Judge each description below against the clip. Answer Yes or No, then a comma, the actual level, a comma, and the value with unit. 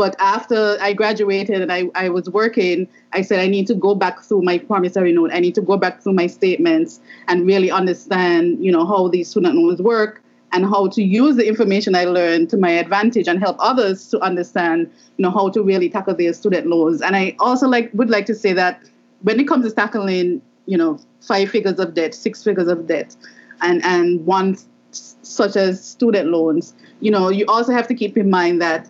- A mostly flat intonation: No, average, 3.3 semitones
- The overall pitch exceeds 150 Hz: Yes, high, 190 Hz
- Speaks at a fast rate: Yes, fast, 220 wpm